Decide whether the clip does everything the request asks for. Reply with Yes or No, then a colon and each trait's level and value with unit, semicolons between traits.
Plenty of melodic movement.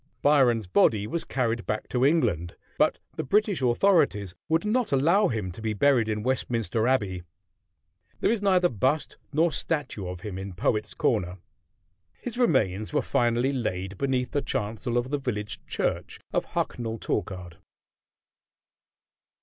Yes: wide, 5.8 semitones